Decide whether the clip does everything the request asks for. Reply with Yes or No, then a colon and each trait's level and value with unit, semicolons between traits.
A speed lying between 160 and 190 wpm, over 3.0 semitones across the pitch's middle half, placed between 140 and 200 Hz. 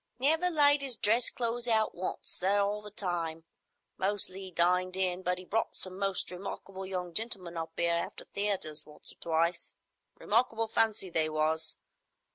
Yes: average, 165 wpm; average, 4.0 semitones; high, 190 Hz